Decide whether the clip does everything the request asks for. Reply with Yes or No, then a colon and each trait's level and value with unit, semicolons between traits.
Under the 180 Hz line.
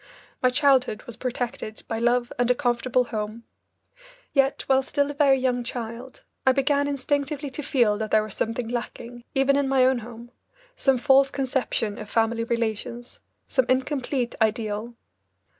No: high, 245 Hz